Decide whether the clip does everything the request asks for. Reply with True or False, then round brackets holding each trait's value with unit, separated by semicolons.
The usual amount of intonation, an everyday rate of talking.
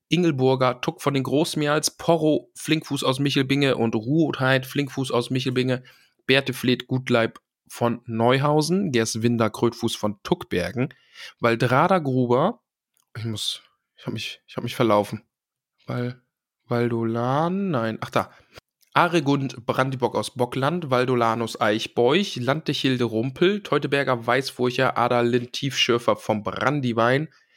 False (3.1 semitones; 115 wpm)